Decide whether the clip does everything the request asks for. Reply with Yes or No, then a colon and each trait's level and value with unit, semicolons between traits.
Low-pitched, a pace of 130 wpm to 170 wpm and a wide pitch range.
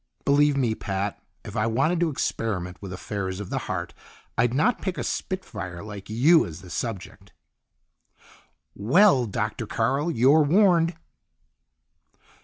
Yes: low, 115 Hz; average, 140 wpm; wide, 7.7 semitones